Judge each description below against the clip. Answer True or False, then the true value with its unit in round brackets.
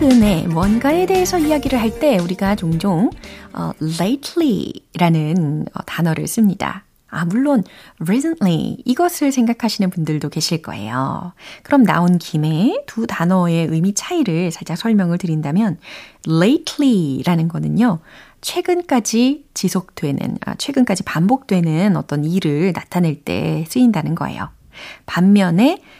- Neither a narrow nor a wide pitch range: False (7.2 semitones)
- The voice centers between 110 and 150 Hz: False (190 Hz)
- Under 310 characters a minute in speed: False (315 characters per minute)